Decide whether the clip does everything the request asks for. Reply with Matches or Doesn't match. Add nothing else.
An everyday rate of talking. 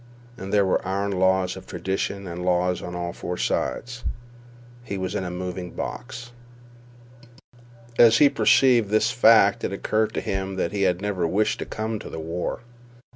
Matches